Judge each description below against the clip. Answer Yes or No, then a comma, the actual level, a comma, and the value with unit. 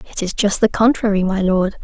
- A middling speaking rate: No, fast, 230 wpm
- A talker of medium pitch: No, high, 200 Hz